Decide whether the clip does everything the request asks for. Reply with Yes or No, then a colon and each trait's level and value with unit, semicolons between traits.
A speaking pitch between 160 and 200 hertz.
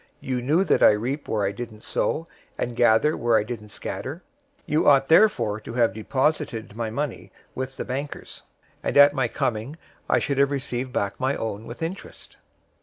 No: low, 125 Hz